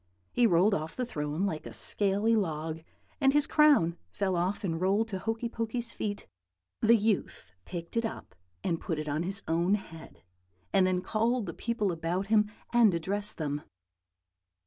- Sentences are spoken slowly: No, average, 170 wpm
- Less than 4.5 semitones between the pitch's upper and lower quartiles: No, average, 5.1 semitones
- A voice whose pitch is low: No, high, 195 Hz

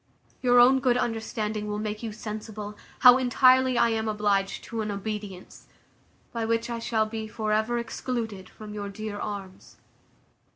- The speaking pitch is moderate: No, high, 220 Hz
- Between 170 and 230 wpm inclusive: No, average, 160 wpm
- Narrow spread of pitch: Yes, narrow, 2.1 semitones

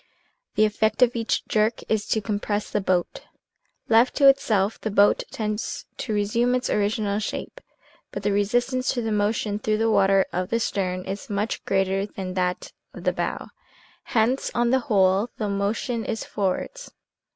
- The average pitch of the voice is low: No, high, 210 Hz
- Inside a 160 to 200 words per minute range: Yes, average, 175 wpm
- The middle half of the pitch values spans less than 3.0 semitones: Yes, narrow, 2.5 semitones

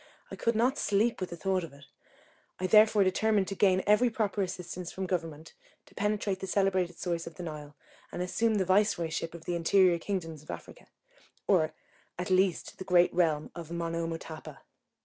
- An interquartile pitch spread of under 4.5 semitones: Yes, average, 3.0 semitones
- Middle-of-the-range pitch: Yes, medium, 180 Hz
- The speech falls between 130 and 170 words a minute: No, average, 180 wpm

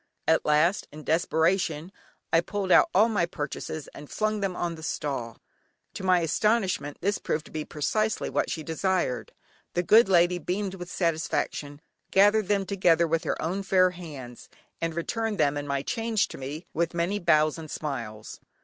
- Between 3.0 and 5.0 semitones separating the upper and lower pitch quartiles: Yes, average, 4.1 semitones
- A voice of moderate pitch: Yes, medium, 170 Hz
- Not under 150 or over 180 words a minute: Yes, average, 175 wpm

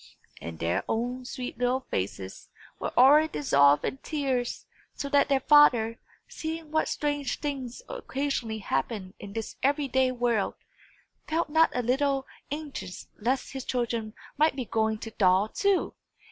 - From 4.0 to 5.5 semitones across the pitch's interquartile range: Yes, average, 4.6 semitones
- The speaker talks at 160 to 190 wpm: No, average, 145 wpm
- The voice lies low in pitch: No, very high, 250 Hz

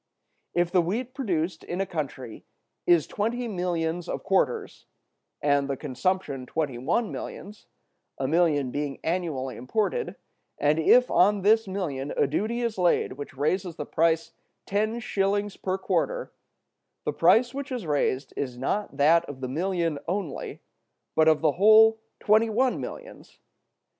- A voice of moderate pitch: Yes, medium, 175 Hz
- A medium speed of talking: Yes, average, 150 wpm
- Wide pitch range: Yes, wide, 6.3 semitones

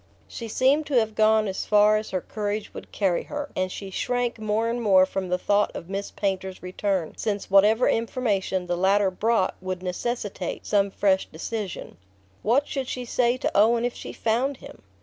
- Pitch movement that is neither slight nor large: Yes, average, 3.5 semitones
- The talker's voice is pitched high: Yes, high, 210 Hz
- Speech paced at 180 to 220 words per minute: Yes, average, 190 wpm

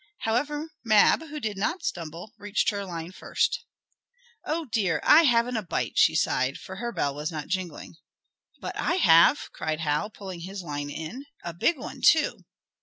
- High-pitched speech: Yes, high, 195 Hz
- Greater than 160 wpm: Yes, average, 175 wpm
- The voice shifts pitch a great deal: Yes, wide, 7.0 semitones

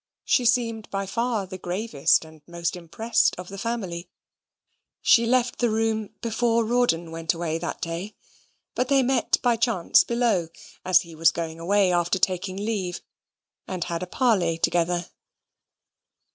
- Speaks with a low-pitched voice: No, high, 190 Hz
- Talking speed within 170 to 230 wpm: No, average, 150 wpm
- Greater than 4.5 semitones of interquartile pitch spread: Yes, average, 5.1 semitones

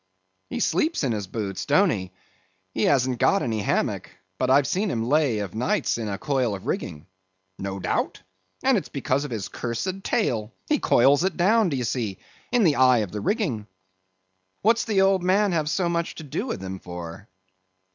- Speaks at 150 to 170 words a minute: No, average, 195 wpm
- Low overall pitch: Yes, low, 130 Hz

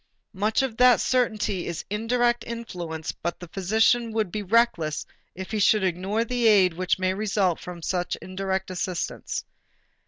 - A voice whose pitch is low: No, high, 195 Hz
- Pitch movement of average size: Yes, average, 3.8 semitones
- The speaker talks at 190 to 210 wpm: No, average, 155 wpm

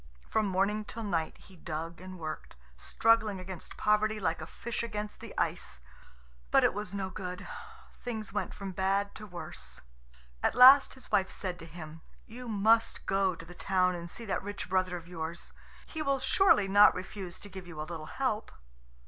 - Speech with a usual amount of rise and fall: Yes, average, 3.3 semitones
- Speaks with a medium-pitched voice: No, high, 195 Hz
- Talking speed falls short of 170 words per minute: No, average, 185 wpm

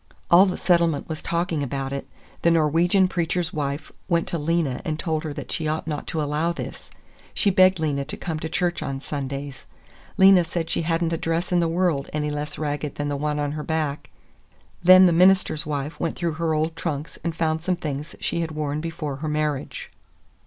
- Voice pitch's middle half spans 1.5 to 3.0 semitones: Yes, narrow, 2.4 semitones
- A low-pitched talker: No, medium, 160 Hz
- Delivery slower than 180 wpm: No, fast, 205 wpm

